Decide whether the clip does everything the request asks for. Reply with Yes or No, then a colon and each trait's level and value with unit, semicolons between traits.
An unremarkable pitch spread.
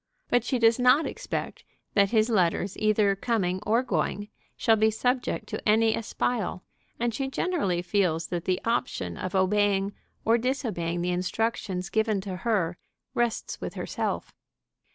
Yes: average, 3.9 semitones